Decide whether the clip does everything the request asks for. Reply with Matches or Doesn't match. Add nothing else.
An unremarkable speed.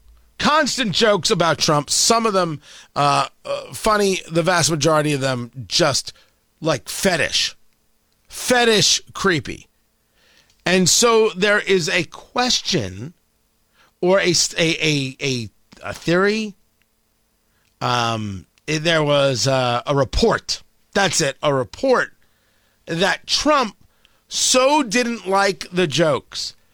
Doesn't match